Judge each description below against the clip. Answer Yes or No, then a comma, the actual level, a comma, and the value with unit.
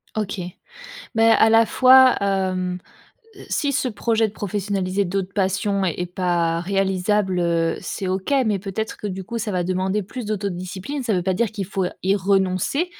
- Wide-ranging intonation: No, average, 2.8 semitones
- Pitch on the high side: Yes, high, 195 Hz